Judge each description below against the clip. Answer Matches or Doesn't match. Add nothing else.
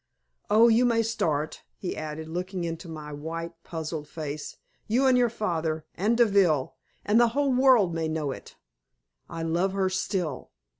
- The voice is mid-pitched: Matches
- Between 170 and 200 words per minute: Doesn't match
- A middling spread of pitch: Doesn't match